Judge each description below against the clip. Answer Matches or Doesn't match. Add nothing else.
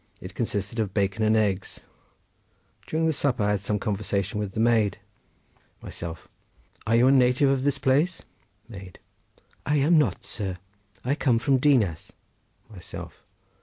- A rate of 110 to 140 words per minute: Matches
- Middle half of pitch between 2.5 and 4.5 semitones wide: Doesn't match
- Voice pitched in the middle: Doesn't match